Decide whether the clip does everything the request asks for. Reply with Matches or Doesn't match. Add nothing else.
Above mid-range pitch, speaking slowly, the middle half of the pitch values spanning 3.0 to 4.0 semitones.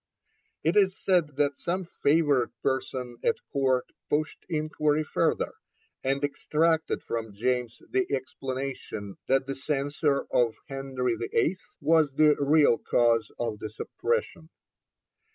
Doesn't match